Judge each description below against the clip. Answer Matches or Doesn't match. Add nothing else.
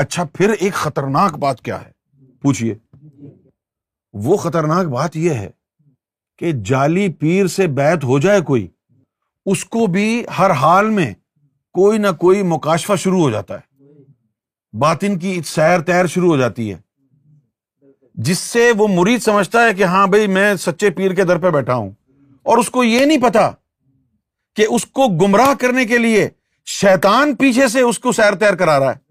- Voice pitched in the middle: Matches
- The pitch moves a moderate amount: Doesn't match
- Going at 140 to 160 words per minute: Doesn't match